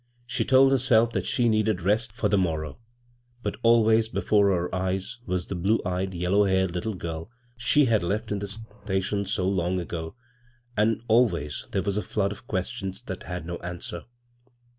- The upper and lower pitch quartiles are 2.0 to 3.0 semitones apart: No, average, 3.6 semitones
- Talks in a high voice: No, low, 100 Hz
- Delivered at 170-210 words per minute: Yes, average, 180 wpm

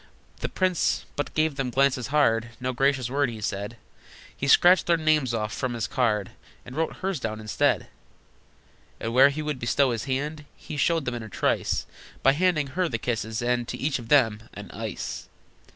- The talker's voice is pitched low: Yes, low, 130 Hz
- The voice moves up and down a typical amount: Yes, average, 4.4 semitones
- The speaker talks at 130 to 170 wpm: No, average, 190 wpm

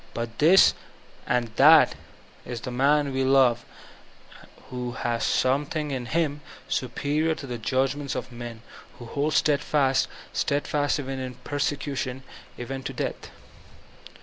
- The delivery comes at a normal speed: No, slow, 120 wpm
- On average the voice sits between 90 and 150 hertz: Yes, low, 135 Hz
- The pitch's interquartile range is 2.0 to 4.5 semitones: Yes, average, 2.8 semitones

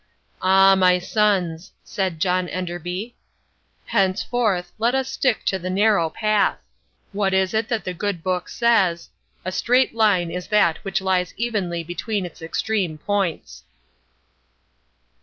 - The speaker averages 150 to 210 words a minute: No, slow, 135 wpm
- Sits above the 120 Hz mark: Yes, high, 190 Hz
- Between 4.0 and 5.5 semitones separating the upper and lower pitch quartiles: No, average, 3.1 semitones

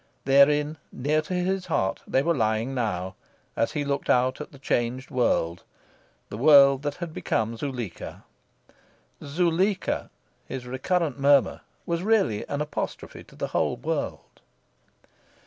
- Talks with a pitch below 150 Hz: Yes, medium, 140 Hz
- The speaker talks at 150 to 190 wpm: No, slow, 135 wpm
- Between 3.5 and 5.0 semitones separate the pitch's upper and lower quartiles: Yes, average, 4.0 semitones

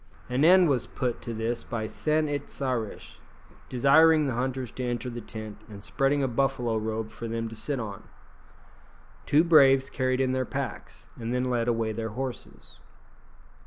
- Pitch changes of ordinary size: Yes, average, 3.1 semitones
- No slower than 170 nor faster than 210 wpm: Yes, average, 175 wpm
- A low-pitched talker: Yes, low, 125 Hz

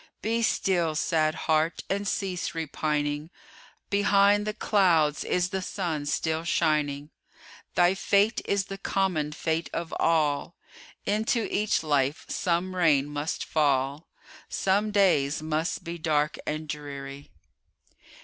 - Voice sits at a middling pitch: Yes, medium, 165 Hz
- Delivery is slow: Yes, slow, 120 wpm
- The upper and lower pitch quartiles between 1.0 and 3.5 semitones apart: No, average, 4.4 semitones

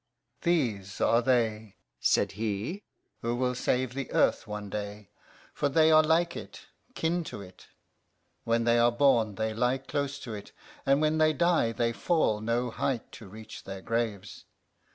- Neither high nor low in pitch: No, low, 120 Hz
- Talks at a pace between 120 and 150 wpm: No, average, 165 wpm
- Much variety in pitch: No, average, 4.8 semitones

